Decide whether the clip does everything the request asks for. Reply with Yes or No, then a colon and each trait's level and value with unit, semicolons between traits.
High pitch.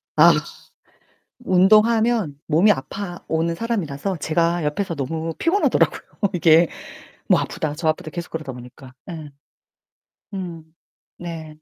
No: medium, 165 Hz